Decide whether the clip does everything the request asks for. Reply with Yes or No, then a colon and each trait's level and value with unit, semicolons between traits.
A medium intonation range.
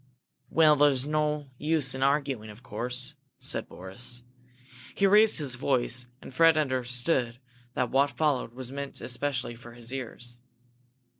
Yes: average, 3.3 semitones